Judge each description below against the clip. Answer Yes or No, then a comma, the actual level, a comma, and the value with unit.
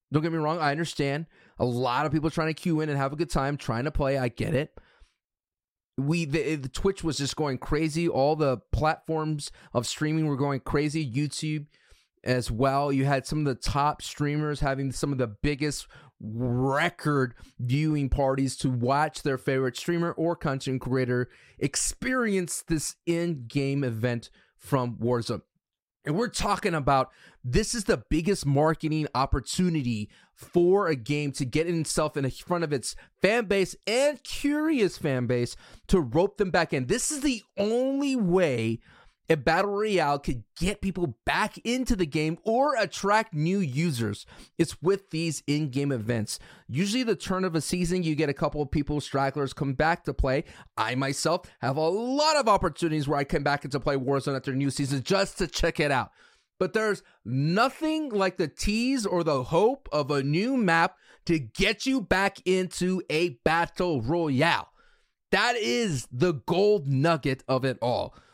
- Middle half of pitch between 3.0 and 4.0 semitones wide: No, average, 4.9 semitones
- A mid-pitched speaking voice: Yes, medium, 155 Hz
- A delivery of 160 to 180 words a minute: Yes, average, 175 wpm